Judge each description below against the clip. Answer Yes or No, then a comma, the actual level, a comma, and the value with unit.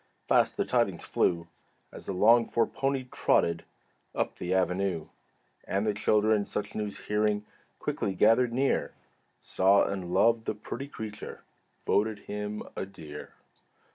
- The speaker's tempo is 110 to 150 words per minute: Yes, average, 140 wpm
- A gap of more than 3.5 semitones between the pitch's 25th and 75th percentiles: No, narrow, 2.6 semitones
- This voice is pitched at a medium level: No, low, 105 Hz